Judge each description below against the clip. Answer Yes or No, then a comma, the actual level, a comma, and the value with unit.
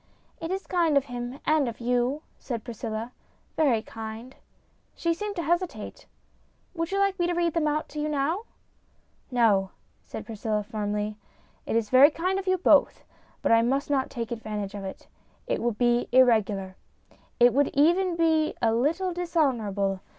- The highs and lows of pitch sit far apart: Yes, wide, 6.8 semitones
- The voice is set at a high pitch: Yes, very high, 260 Hz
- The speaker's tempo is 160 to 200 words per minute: Yes, average, 180 wpm